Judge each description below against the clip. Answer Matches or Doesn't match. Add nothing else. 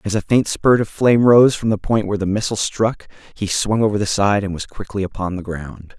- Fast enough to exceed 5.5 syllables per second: Matches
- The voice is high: Doesn't match